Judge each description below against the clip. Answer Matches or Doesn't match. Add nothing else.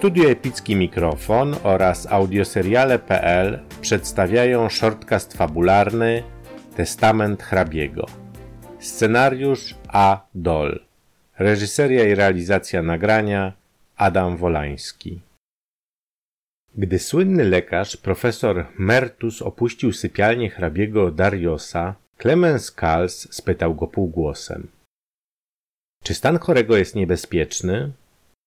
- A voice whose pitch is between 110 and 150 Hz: Doesn't match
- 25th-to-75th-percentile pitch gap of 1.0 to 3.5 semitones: Doesn't match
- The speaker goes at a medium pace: Doesn't match